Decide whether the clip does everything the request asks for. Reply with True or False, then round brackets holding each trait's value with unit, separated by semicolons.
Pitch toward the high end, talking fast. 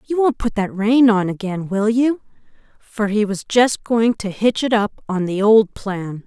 True (215 Hz; 210 wpm)